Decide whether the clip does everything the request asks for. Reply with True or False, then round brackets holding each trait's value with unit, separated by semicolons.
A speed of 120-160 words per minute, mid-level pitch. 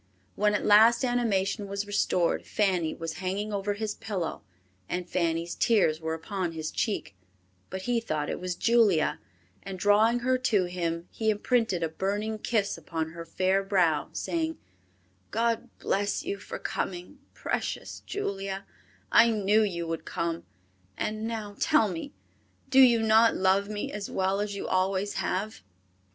False (155 wpm; 200 Hz)